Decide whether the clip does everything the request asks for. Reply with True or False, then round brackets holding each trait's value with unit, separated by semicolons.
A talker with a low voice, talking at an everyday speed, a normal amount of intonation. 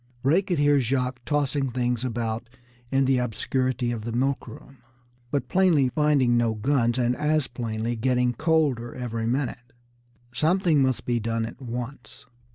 True (125 Hz; 155 wpm; 3.0 semitones)